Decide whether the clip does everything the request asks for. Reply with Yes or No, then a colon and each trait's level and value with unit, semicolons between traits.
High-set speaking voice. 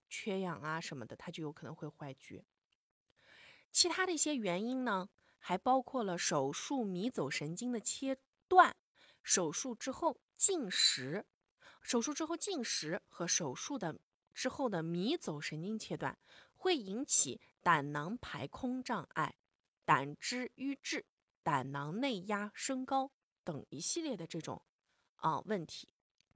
Yes: high, 225 Hz